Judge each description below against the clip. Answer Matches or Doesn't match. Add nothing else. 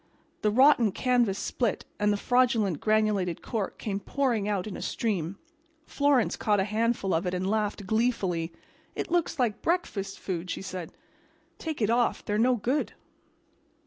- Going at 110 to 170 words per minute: Matches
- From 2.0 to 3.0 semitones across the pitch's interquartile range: Doesn't match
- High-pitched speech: Matches